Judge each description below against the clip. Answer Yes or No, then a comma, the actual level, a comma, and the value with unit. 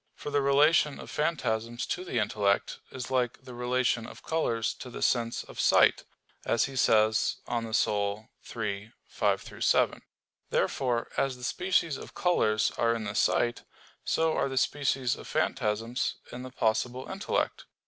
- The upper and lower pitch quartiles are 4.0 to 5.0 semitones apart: No, average, 3.4 semitones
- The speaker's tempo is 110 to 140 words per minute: No, average, 155 wpm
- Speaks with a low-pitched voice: Yes, low, 120 Hz